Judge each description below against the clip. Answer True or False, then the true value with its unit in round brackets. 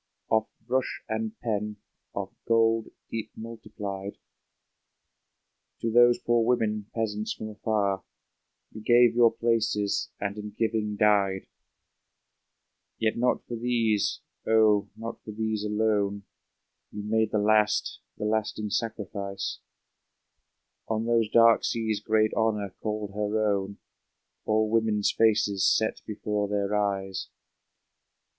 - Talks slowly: True (115 wpm)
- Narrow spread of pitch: True (1.5 semitones)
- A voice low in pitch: True (110 Hz)